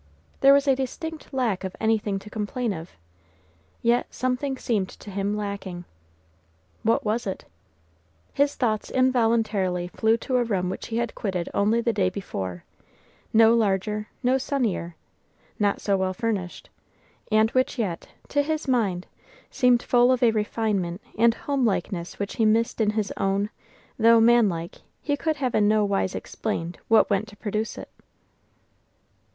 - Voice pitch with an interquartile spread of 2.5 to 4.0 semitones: Yes, average, 3.6 semitones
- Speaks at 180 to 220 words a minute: No, average, 155 wpm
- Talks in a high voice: Yes, high, 220 Hz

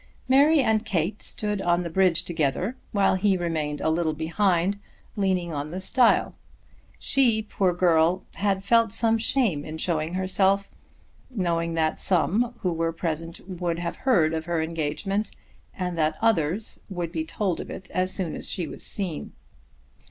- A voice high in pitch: No, medium, 180 Hz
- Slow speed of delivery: No, average, 160 wpm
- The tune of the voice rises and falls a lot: No, average, 3.7 semitones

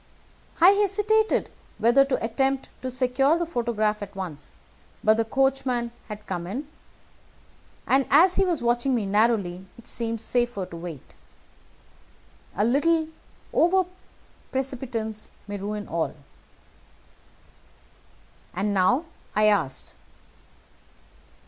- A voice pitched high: Yes, high, 235 Hz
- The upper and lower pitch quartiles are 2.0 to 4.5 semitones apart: No, average, 4.9 semitones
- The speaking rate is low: Yes, slow, 110 wpm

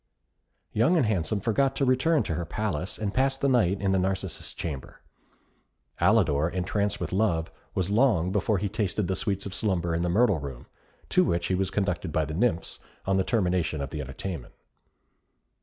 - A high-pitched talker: No, very low, 95 Hz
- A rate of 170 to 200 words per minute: Yes, average, 185 wpm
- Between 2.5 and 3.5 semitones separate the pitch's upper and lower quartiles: No, average, 4.1 semitones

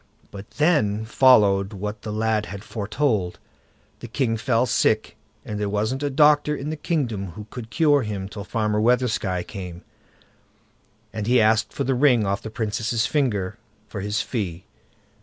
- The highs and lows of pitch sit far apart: No, average, 3.6 semitones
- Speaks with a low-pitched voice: Yes, low, 110 Hz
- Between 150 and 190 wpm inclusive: Yes, average, 160 wpm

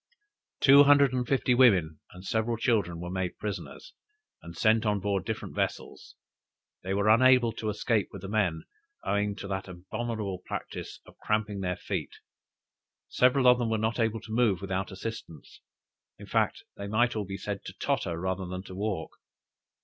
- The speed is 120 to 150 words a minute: No, average, 170 wpm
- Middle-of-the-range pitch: No, low, 105 Hz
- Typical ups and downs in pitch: Yes, average, 3.3 semitones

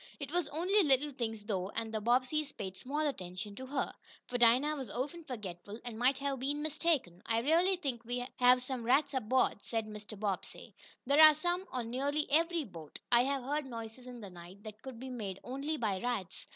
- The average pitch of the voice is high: Yes, very high, 250 Hz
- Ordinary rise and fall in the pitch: Yes, average, 4.8 semitones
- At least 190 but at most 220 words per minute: Yes, fast, 205 wpm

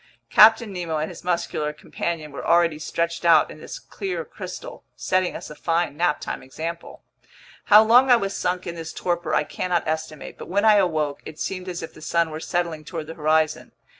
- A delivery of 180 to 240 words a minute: Yes, average, 195 wpm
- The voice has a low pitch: No, medium, 170 Hz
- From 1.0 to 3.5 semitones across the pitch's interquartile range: Yes, average, 2.7 semitones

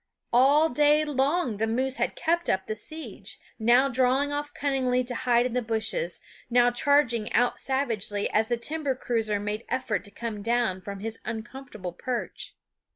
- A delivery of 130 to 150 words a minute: No, average, 165 wpm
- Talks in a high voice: Yes, high, 245 Hz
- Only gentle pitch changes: No, average, 3.7 semitones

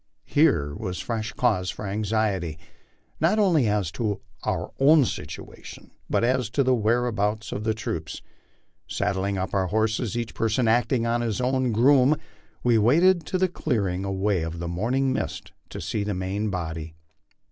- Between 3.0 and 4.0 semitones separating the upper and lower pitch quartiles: No, average, 4.6 semitones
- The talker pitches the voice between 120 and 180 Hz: No, low, 110 Hz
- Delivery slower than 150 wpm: No, average, 160 wpm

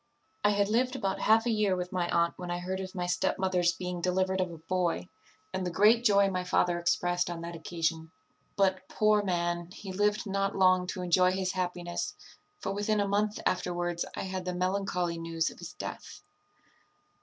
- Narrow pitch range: Yes, narrow, 2.1 semitones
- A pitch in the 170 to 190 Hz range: Yes, medium, 185 Hz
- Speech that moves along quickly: No, average, 190 wpm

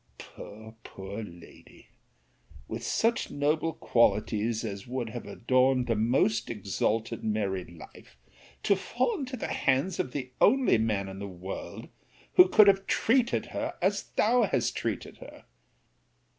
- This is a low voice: Yes, low, 120 Hz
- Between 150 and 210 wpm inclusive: No, average, 140 wpm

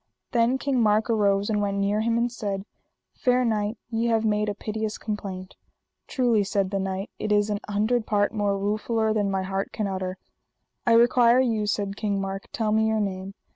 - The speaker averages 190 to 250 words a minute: Yes, average, 195 wpm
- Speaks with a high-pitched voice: Yes, high, 210 Hz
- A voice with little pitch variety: Yes, narrow, 2.2 semitones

